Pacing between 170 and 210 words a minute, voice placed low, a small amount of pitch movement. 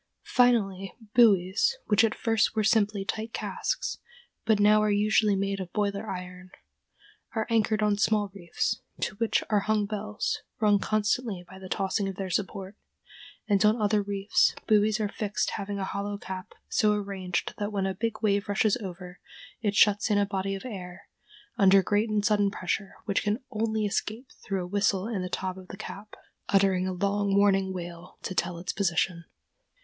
No: average, 180 wpm; high, 200 Hz; narrow, 2.0 semitones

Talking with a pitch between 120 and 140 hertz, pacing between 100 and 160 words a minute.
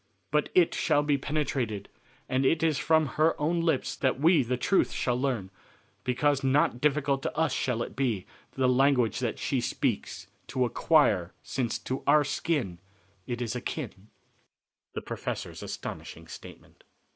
Yes: low, 135 Hz; average, 155 wpm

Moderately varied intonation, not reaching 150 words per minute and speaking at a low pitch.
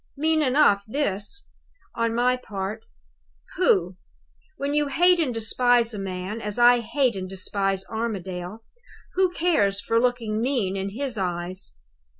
No: average, 5.0 semitones; average, 140 wpm; high, 225 Hz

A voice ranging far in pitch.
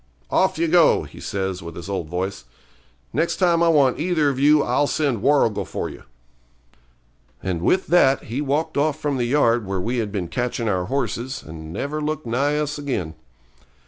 Yes: wide, 7.3 semitones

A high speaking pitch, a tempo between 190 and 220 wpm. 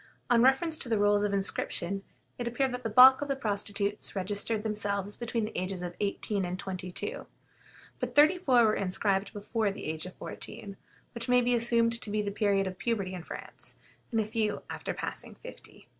Yes: high, 210 Hz; average, 200 wpm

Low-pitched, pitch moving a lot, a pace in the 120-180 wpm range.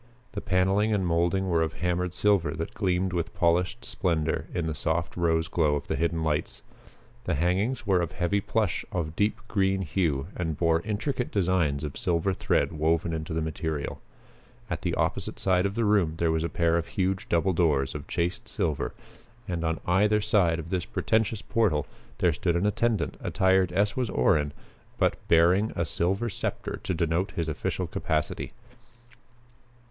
No: very low, 85 Hz; average, 3.1 semitones; average, 175 wpm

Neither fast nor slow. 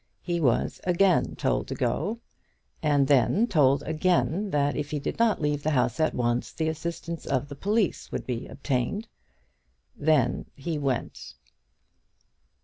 Yes: average, 145 wpm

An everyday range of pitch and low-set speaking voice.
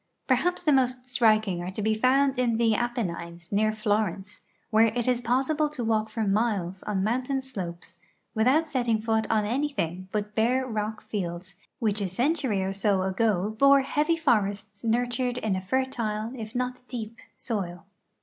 No: average, 3.8 semitones; high, 220 Hz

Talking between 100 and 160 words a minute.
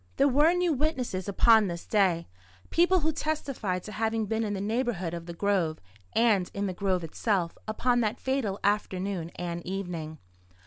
No: average, 170 wpm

